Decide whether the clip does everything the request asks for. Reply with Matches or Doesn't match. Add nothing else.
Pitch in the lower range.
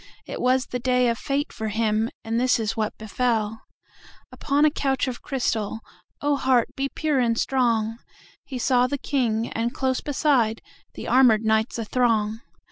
Doesn't match